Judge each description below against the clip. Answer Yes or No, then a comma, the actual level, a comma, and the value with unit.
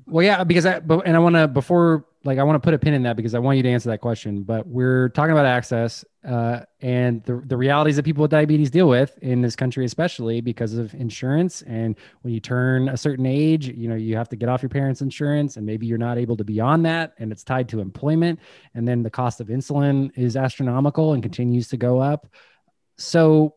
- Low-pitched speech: Yes, low, 130 Hz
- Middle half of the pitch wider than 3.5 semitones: Yes, average, 4.1 semitones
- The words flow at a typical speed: No, fast, 240 wpm